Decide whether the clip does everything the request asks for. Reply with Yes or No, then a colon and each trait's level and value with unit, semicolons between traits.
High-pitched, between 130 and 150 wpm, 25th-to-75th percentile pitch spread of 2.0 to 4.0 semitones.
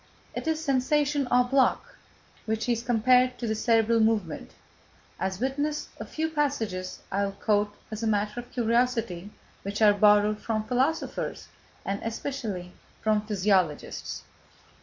Yes: high, 225 Hz; average, 140 wpm; average, 3.6 semitones